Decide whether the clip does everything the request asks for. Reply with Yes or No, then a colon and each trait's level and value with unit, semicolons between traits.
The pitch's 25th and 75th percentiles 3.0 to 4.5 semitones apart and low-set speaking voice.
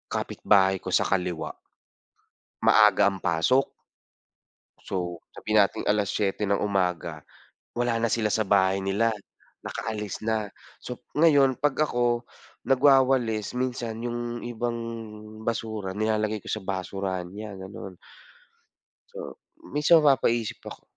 Yes: average, 3.7 semitones; low, 110 Hz